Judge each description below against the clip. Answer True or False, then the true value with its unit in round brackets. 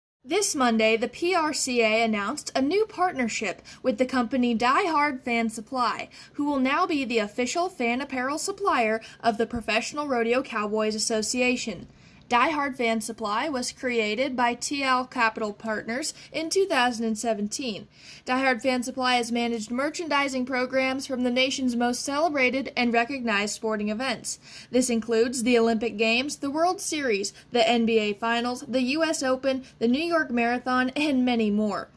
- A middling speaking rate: True (150 wpm)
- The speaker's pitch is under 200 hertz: False (250 Hz)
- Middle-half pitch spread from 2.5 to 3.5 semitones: True (3.1 semitones)